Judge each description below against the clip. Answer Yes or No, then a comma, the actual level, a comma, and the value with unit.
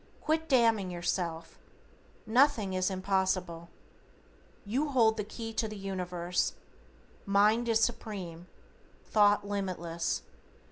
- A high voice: Yes, high, 200 Hz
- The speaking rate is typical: No, slow, 100 wpm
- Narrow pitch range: No, average, 3.8 semitones